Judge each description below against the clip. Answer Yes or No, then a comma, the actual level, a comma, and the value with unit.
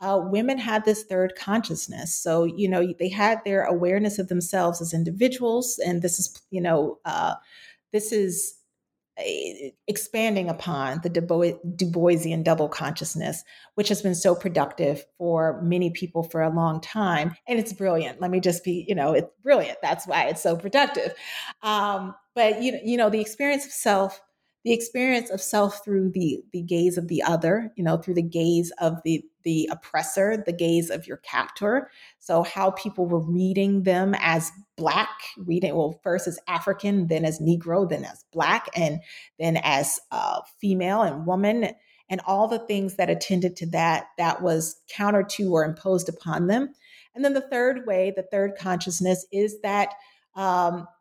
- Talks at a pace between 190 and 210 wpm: No, average, 175 wpm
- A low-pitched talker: No, medium, 185 Hz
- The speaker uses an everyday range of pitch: Yes, average, 3.6 semitones